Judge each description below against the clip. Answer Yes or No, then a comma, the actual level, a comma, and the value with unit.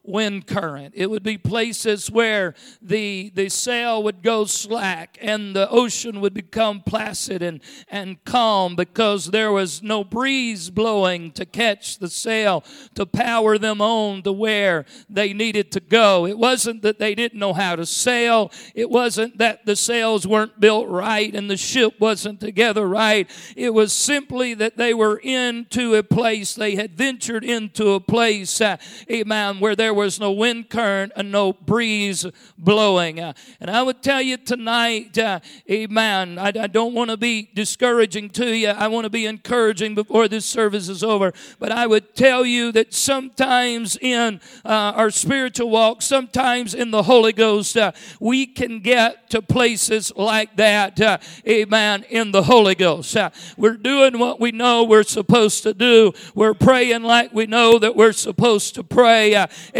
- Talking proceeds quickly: No, average, 175 wpm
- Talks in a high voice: Yes, high, 220 Hz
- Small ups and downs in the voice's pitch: Yes, narrow, 2.3 semitones